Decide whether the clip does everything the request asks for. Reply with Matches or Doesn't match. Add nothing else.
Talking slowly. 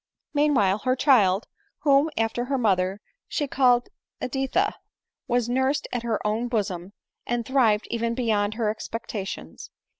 Matches